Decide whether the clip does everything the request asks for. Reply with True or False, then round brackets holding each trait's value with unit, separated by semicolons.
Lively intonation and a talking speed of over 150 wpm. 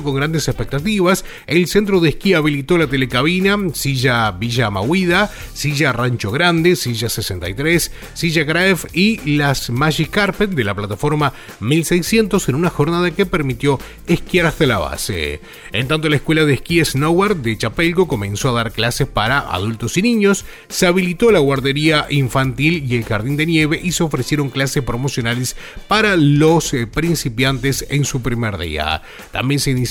True (5.8 semitones; 160 wpm)